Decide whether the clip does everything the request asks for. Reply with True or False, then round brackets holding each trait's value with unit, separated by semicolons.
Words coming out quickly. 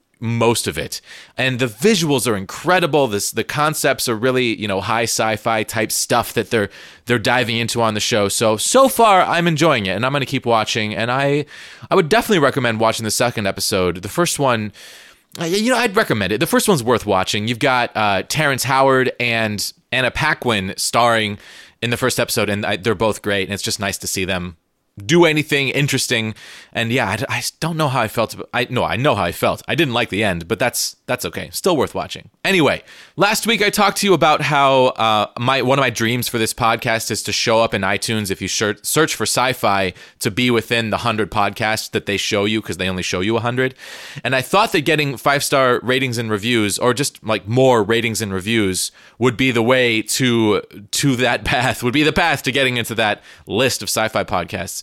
True (220 wpm)